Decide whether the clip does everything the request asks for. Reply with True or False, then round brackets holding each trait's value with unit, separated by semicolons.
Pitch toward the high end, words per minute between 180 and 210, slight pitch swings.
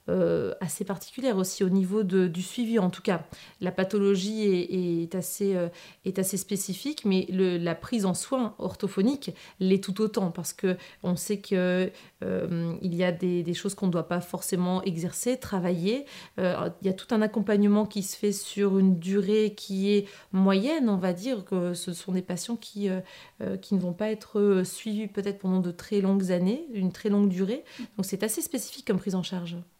True (195 Hz; 200 wpm; 2.3 semitones)